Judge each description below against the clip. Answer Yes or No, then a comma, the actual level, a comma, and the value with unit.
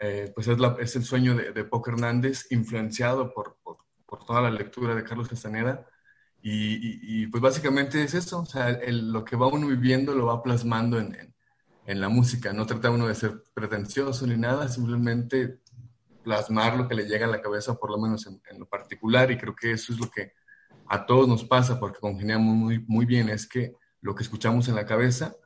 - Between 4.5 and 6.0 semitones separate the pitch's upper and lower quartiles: No, narrow, 2.4 semitones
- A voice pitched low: Yes, low, 120 Hz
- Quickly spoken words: Yes, fast, 220 wpm